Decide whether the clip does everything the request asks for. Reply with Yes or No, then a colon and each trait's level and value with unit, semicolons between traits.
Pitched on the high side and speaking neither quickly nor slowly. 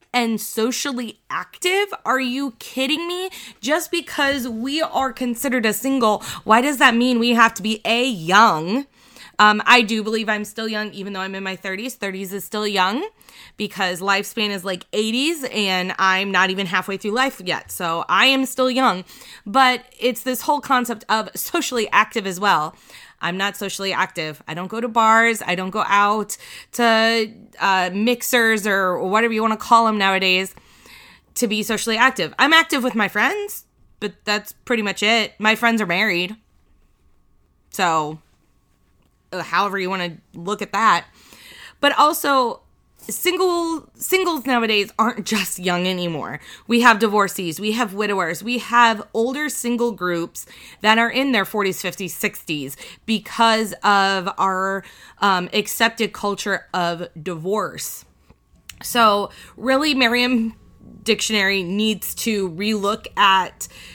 Yes: high, 215 Hz; average, 150 wpm